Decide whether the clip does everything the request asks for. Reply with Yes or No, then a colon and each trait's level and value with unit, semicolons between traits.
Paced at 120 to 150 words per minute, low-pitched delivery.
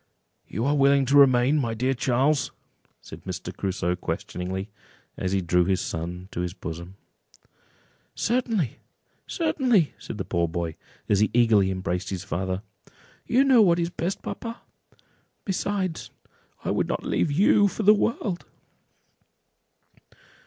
Yes: average, 140 wpm; low, 125 Hz